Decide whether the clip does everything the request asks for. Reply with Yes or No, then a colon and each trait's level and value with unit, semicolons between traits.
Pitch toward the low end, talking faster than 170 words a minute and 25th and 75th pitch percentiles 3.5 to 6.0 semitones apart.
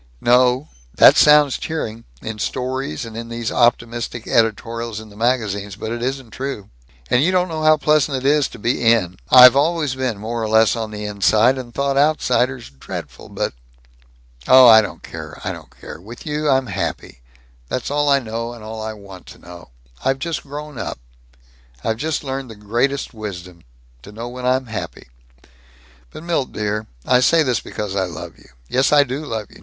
Yes: low, 120 Hz; average, 190 wpm; average, 3.8 semitones